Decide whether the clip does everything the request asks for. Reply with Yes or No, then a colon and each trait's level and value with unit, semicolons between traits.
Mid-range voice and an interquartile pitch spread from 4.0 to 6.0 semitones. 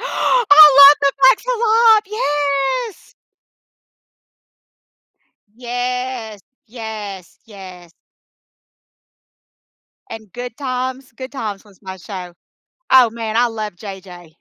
No: high, 245 Hz; average, 5.2 semitones